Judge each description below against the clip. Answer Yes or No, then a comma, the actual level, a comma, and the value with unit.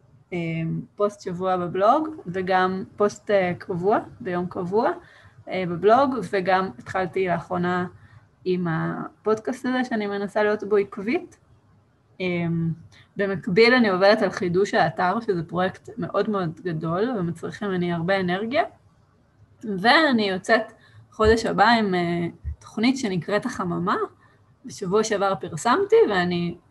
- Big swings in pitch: No, average, 3.4 semitones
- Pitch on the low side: No, high, 190 Hz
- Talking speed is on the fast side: No, average, 105 wpm